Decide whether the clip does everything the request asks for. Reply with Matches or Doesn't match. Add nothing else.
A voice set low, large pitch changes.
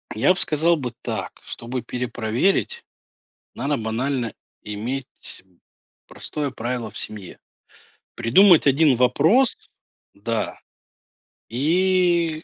Matches